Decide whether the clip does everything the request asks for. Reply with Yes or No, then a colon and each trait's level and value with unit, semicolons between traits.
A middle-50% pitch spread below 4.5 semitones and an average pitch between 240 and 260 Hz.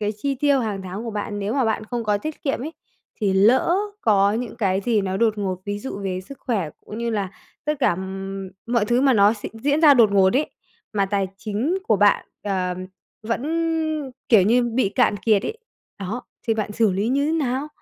No: average, 3.9 semitones; high, 215 Hz